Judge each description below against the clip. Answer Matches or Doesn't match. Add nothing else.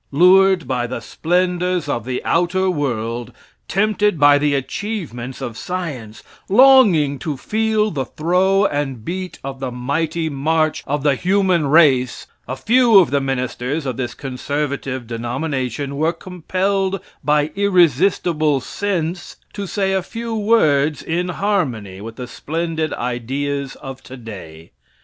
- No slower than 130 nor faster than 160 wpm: Matches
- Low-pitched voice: Doesn't match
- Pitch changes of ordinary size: Doesn't match